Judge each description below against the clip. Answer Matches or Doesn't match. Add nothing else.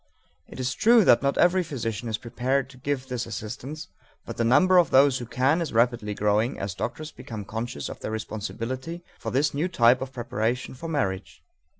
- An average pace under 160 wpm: Doesn't match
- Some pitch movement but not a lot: Matches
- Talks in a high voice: Doesn't match